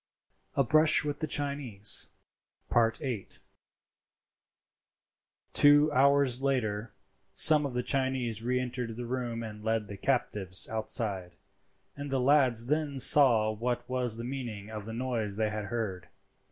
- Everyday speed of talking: No, slow, 130 wpm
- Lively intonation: No, average, 3.8 semitones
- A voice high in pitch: No, low, 120 Hz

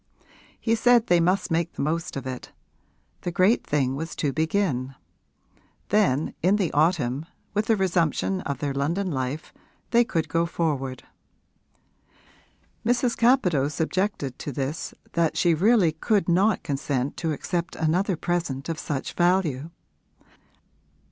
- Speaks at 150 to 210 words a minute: No, slow, 135 wpm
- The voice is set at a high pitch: No, medium, 165 Hz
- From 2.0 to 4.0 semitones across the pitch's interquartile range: No, average, 4.9 semitones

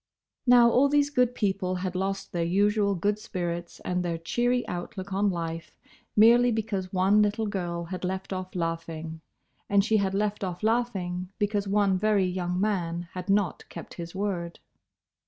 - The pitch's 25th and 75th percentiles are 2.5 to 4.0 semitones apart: Yes, average, 2.9 semitones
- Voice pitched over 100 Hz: Yes, high, 190 Hz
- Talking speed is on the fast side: No, average, 165 wpm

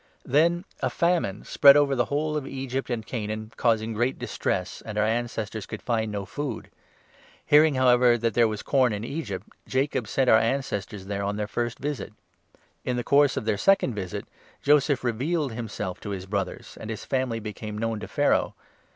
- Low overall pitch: Yes, low, 120 Hz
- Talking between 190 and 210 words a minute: Yes, average, 195 wpm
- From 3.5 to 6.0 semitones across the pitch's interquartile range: Yes, average, 4.1 semitones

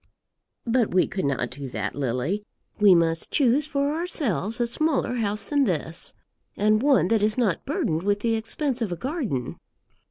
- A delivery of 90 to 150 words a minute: No, average, 170 wpm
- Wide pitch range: Yes, wide, 7.3 semitones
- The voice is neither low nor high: No, high, 215 Hz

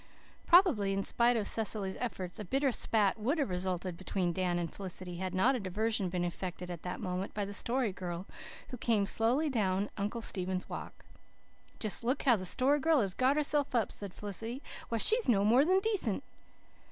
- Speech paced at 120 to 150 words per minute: No, average, 190 wpm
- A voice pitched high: Yes, high, 210 Hz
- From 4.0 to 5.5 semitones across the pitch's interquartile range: Yes, average, 5.2 semitones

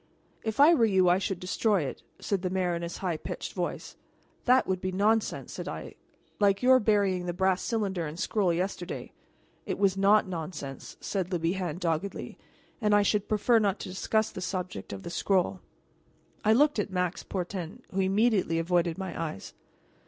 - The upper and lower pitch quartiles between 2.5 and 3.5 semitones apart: Yes, average, 2.8 semitones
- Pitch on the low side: No, high, 190 Hz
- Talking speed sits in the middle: Yes, average, 180 wpm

